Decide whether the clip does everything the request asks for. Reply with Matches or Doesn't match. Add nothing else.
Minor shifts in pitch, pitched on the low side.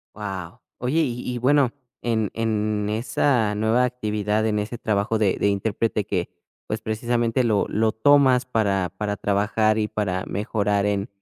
Matches